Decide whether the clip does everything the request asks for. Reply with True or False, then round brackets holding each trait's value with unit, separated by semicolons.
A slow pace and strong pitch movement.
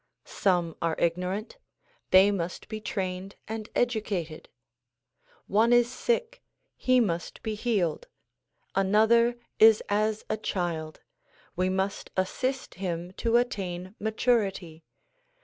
False (110 wpm; 4.0 semitones)